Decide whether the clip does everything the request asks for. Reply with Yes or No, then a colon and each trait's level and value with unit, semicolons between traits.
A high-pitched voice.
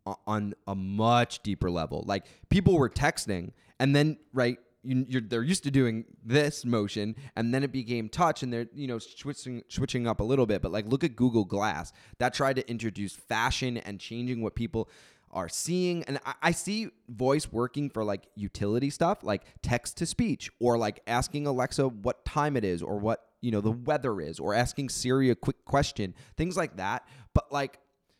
No: low, 120 Hz